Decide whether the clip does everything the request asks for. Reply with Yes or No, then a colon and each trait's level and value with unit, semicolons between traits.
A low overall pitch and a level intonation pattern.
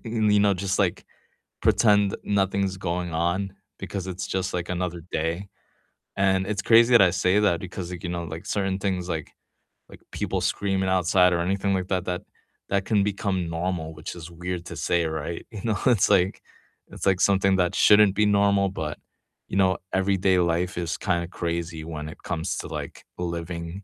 Yes: very low, 95 Hz; narrow, 2.3 semitones